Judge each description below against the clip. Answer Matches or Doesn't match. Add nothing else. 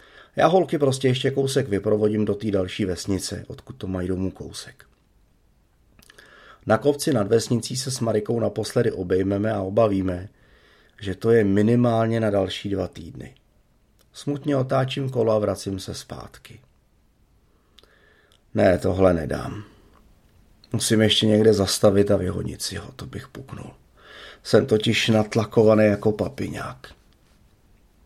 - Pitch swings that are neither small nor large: Matches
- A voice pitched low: Matches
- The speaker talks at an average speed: Matches